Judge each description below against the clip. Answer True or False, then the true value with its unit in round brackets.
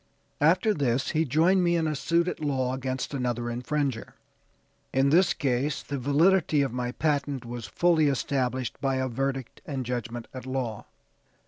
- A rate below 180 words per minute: True (160 wpm)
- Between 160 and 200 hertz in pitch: False (135 Hz)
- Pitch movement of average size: True (3.3 semitones)